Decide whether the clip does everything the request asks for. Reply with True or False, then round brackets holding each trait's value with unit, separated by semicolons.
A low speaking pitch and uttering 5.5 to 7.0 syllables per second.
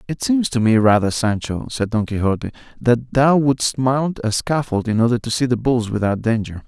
False (120 Hz; 5.0 syllables/s)